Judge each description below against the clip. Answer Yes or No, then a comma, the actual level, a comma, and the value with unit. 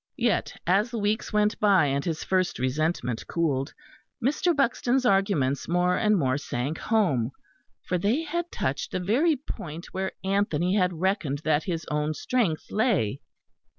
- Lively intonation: Yes, wide, 5.9 semitones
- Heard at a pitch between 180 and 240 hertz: Yes, medium, 185 Hz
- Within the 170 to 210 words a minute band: No, average, 150 wpm